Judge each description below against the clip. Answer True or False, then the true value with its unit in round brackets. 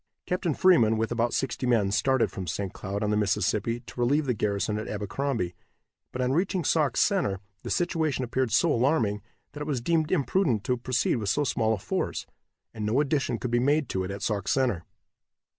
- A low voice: True (120 Hz)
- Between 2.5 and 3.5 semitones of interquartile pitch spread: False (5.4 semitones)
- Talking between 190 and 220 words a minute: True (200 wpm)